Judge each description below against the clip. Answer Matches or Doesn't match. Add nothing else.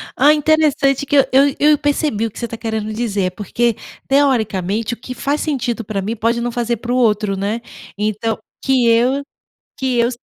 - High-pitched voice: Matches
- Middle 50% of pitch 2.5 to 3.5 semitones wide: Doesn't match